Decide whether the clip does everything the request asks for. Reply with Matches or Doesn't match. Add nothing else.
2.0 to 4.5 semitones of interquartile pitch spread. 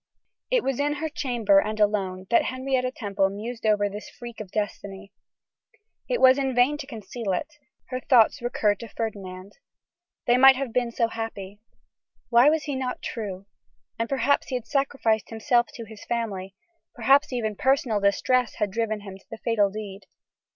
Matches